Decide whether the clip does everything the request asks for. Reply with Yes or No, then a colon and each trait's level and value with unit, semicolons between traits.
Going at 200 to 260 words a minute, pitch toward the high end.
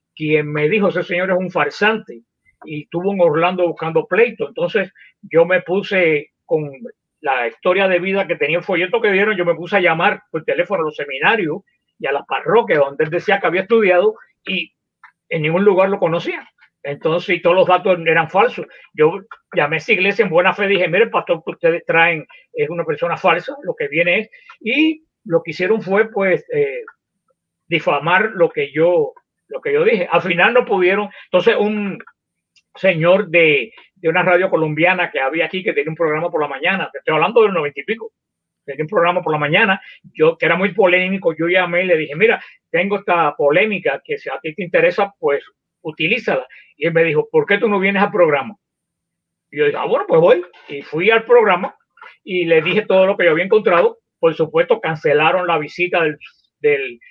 Yes: fast, 205 wpm; high, 200 Hz